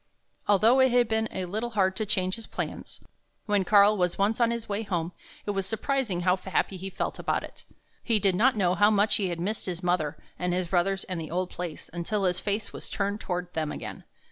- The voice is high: Yes, high, 195 Hz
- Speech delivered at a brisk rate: Yes, fast, 225 wpm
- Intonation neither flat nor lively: Yes, average, 3.2 semitones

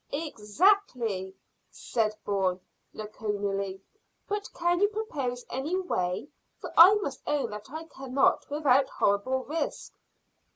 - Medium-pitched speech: No, very high, 260 Hz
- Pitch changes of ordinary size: No, wide, 7.9 semitones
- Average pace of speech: No, slow, 115 wpm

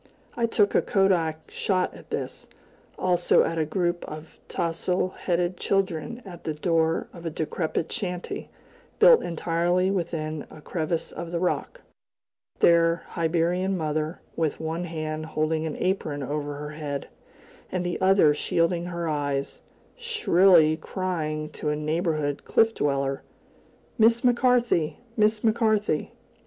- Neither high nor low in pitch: Yes, medium, 170 Hz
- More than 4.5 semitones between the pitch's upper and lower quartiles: No, average, 3.1 semitones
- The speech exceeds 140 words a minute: No, slow, 135 wpm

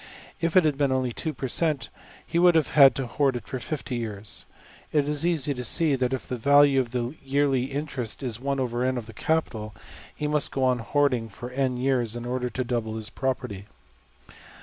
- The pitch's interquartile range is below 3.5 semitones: Yes, average, 3.0 semitones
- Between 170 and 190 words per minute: Yes, average, 180 wpm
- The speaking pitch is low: Yes, low, 130 Hz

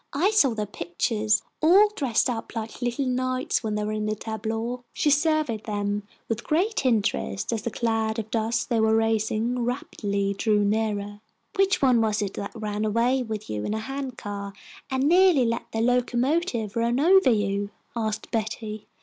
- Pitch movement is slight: No, average, 3.1 semitones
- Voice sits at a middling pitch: No, high, 225 Hz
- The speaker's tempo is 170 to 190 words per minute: Yes, average, 175 wpm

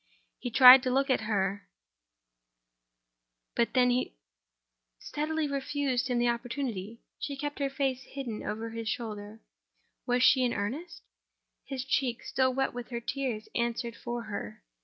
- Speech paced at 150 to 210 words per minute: No, average, 140 wpm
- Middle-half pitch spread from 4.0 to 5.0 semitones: Yes, average, 4.4 semitones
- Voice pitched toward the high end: Yes, high, 240 Hz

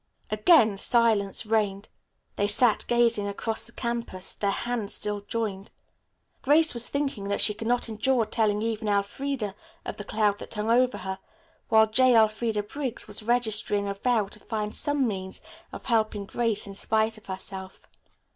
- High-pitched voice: Yes, high, 220 Hz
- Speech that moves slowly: No, average, 165 wpm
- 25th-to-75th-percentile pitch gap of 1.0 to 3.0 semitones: Yes, average, 2.7 semitones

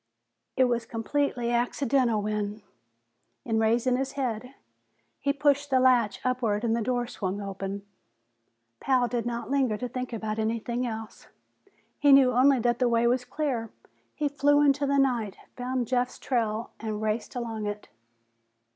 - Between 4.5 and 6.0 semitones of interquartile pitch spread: No, average, 2.8 semitones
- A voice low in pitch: No, high, 240 Hz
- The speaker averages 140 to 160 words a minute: Yes, average, 155 wpm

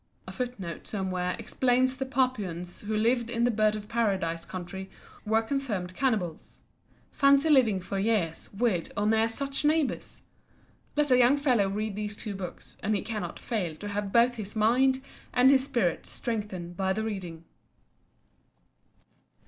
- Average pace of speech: Yes, average, 155 wpm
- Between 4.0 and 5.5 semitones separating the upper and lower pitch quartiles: Yes, average, 4.7 semitones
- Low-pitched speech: No, high, 215 Hz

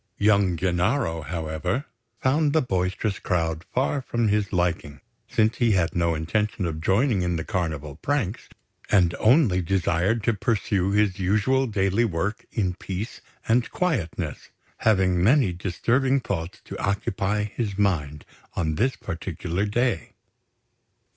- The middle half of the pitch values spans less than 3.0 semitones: No, average, 4.4 semitones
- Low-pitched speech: Yes, very low, 95 Hz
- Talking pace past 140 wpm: No, slow, 135 wpm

